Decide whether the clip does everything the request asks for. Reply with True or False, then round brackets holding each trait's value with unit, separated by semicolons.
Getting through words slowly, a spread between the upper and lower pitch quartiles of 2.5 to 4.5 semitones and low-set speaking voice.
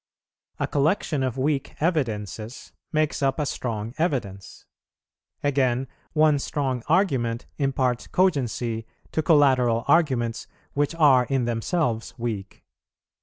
True (110 wpm; 4.2 semitones; 130 Hz)